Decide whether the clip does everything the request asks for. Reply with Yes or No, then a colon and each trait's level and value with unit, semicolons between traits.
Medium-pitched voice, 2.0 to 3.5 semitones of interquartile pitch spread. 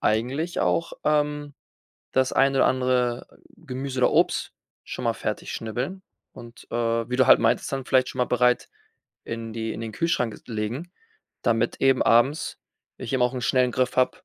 No: low, 125 Hz; narrow, 2.4 semitones